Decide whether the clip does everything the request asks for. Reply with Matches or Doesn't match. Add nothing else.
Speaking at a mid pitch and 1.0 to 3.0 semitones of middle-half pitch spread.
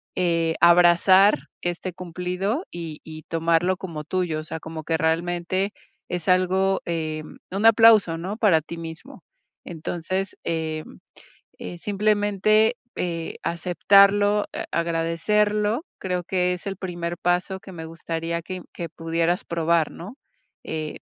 Matches